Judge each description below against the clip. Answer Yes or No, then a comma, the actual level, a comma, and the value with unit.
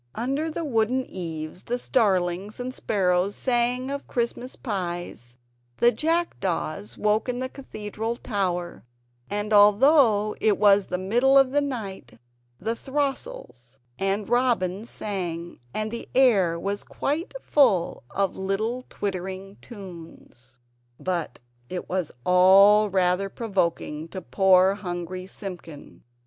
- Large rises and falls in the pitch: No, average, 4.9 semitones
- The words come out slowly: Yes, slow, 120 wpm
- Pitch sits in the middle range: No, high, 200 Hz